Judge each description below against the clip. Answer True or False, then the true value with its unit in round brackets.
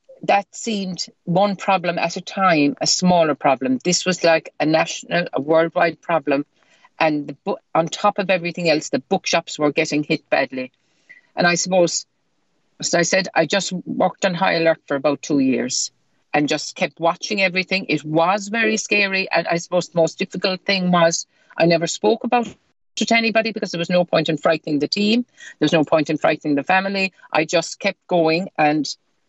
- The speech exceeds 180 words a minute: True (195 wpm)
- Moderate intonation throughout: True (3.7 semitones)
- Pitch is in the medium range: True (170 Hz)